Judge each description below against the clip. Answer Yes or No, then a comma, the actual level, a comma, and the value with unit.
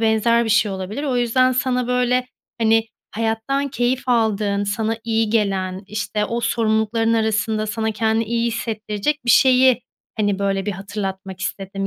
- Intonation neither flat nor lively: No, narrow, 2.3 semitones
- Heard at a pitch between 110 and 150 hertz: No, high, 220 Hz